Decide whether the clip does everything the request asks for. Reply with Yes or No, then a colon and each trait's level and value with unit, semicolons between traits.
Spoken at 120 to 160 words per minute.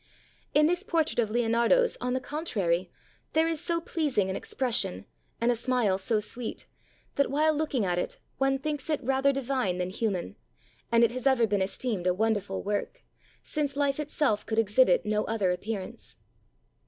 No: average, 175 wpm